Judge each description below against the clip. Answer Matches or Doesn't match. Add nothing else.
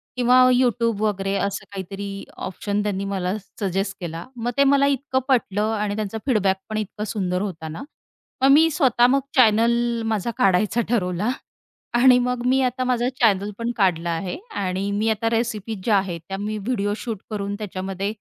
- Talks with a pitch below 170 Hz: Doesn't match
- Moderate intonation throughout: Matches